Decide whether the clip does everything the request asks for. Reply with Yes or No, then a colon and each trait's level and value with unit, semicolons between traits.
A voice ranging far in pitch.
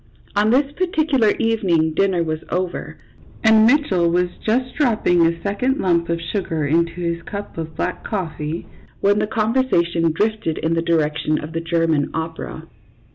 No: average, 4.8 semitones